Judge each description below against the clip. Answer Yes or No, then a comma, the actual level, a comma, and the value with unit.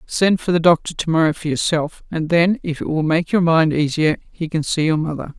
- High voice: No, medium, 160 Hz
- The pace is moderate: No, fast, 245 wpm